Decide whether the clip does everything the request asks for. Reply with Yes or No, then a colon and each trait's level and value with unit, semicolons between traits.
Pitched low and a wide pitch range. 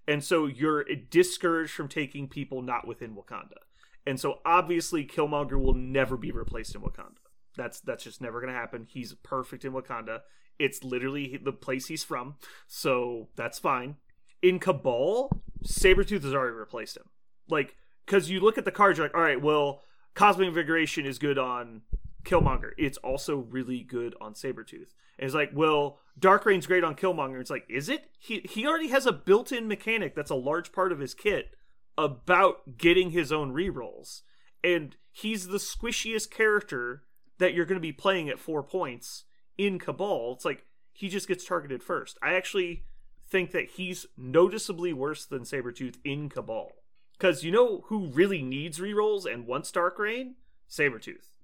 No: medium, 165 Hz; wide, 6.2 semitones